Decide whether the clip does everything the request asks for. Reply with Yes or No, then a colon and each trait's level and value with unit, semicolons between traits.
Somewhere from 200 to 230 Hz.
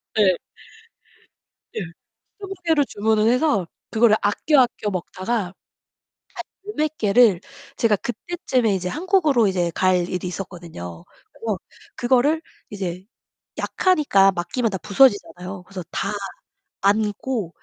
Yes: high, 210 Hz